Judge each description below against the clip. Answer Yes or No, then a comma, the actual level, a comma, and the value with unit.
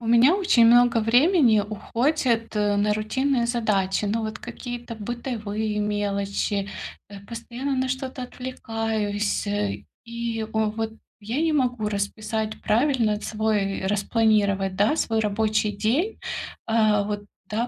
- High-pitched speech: Yes, high, 220 Hz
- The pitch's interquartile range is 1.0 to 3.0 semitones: Yes, narrow, 2.6 semitones